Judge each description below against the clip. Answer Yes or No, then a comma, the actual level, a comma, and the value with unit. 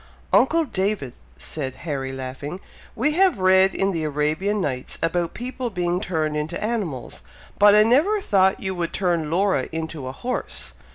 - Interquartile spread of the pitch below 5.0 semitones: No, wide, 5.6 semitones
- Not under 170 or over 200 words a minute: No, average, 160 wpm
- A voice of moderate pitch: Yes, medium, 180 Hz